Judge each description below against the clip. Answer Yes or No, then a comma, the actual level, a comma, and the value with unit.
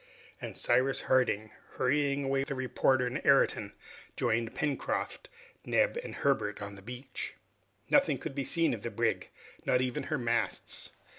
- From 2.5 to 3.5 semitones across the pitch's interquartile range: Yes, average, 2.9 semitones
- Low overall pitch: Yes, low, 130 Hz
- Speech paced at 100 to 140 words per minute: No, average, 150 wpm